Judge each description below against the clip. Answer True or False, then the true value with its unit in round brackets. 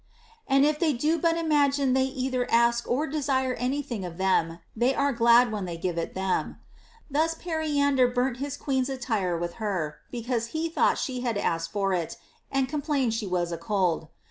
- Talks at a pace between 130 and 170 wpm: False (190 wpm)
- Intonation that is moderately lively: False (6.3 semitones)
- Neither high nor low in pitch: False (250 Hz)